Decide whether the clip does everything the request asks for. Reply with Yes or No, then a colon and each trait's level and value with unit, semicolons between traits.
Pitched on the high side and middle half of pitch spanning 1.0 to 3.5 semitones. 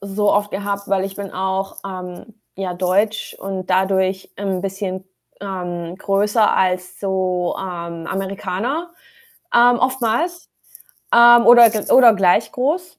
Yes: high, 195 Hz; average, 3.0 semitones